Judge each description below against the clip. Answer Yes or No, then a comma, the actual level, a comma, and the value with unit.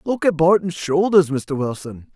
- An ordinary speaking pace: Yes, average, 165 wpm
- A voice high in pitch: No, medium, 165 Hz